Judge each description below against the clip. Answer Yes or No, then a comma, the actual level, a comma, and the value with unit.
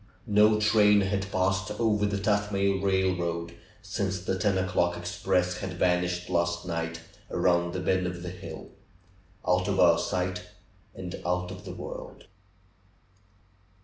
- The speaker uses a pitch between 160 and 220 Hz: No, very low, 95 Hz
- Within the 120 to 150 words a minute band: Yes, average, 145 wpm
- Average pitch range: No, narrow, 1.8 semitones